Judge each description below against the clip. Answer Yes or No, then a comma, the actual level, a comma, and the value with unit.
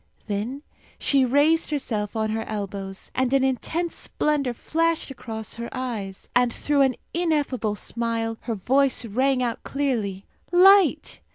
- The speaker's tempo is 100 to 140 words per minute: Yes, slow, 135 wpm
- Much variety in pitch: No, average, 4.4 semitones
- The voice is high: Yes, very high, 250 Hz